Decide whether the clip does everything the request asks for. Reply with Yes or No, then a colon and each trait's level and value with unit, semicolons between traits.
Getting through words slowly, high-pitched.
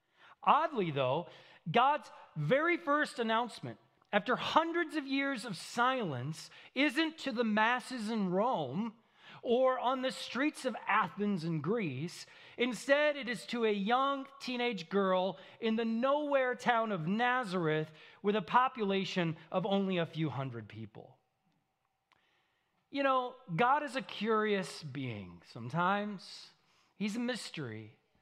Yes: slow, 130 wpm; high, 225 Hz